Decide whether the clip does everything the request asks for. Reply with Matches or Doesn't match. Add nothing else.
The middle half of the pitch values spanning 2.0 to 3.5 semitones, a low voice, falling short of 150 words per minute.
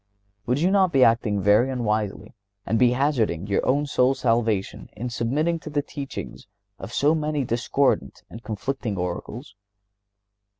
Doesn't match